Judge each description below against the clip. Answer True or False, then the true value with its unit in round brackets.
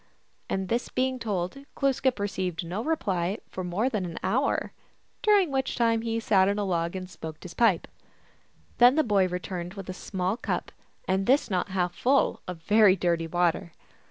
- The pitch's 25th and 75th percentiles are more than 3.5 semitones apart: True (4.6 semitones)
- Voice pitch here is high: True (195 Hz)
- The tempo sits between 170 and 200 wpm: True (180 wpm)